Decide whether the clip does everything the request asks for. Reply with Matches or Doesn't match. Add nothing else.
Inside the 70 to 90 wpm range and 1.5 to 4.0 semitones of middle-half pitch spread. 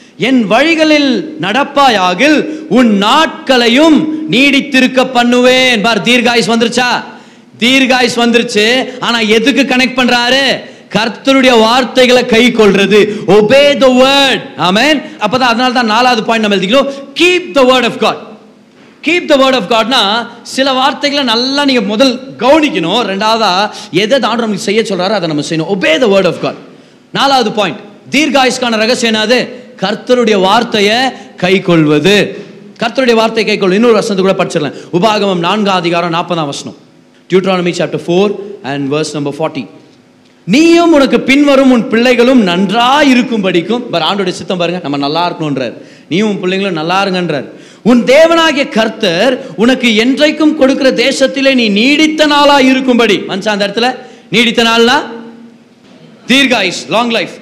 Doesn't match